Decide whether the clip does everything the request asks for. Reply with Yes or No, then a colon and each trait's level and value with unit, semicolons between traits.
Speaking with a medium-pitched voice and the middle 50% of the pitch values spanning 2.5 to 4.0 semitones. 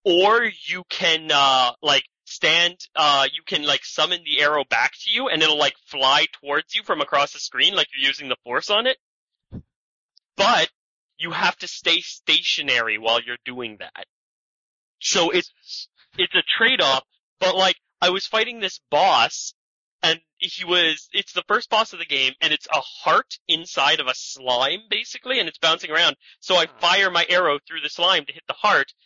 No: medium, 175 Hz; average, 4.6 semitones